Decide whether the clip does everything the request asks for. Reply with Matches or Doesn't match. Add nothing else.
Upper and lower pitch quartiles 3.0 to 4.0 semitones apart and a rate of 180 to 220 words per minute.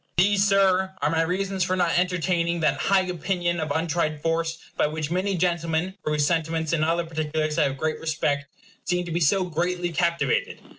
Doesn't match